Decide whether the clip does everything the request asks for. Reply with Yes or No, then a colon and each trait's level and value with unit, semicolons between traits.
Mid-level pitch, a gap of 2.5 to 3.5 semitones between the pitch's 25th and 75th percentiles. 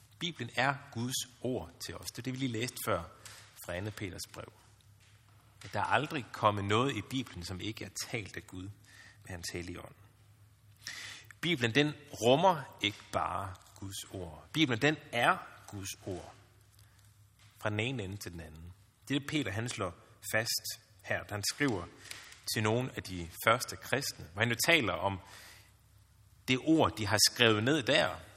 No: low, 105 Hz; average, 3.2 semitones